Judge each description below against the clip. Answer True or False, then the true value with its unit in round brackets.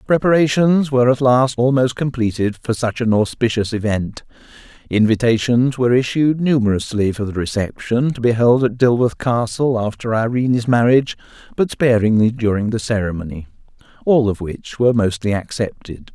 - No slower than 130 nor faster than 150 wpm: True (140 wpm)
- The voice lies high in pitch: False (120 Hz)